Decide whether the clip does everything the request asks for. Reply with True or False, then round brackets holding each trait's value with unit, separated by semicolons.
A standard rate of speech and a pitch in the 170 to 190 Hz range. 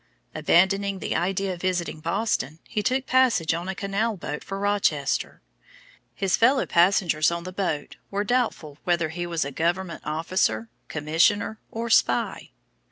True (150 wpm; 185 Hz)